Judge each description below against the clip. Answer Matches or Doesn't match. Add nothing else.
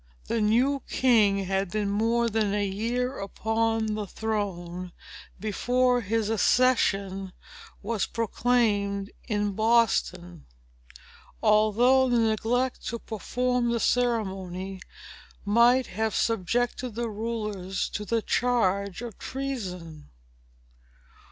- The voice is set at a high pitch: Matches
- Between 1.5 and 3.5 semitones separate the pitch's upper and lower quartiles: Matches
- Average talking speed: Doesn't match